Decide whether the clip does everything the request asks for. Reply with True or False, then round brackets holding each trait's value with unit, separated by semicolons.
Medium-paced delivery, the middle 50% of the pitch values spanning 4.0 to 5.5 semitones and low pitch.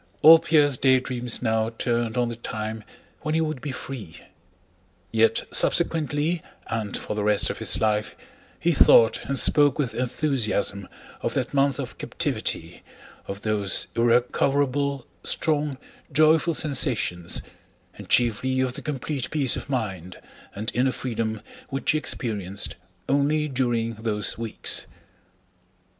False (130 wpm; 4.3 semitones; 125 Hz)